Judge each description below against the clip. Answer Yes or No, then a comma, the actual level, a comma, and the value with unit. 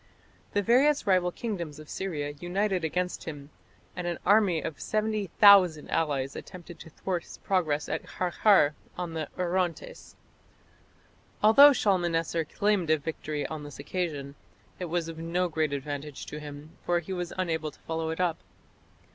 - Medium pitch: Yes, medium, 170 Hz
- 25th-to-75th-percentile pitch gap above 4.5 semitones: No, average, 3.4 semitones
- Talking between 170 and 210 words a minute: No, average, 155 wpm